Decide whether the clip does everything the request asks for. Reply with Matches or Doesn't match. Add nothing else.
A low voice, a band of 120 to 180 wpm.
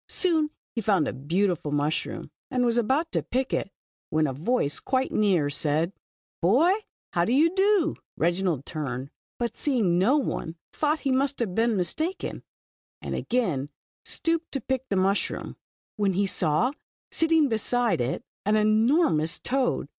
Doesn't match